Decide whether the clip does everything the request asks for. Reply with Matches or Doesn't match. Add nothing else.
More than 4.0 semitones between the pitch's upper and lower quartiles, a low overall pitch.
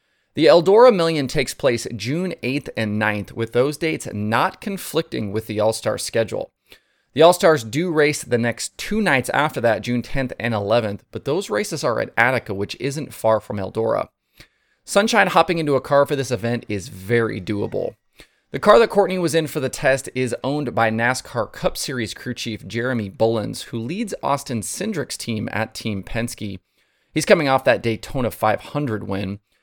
Matches